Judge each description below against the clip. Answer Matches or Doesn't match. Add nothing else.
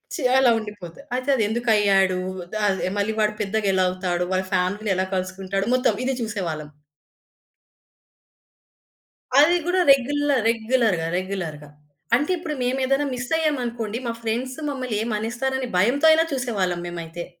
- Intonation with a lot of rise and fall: Matches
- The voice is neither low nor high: Doesn't match